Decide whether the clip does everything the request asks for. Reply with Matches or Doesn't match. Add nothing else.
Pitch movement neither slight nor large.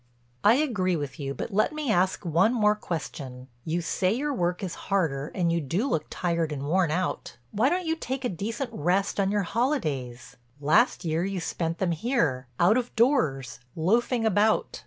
Doesn't match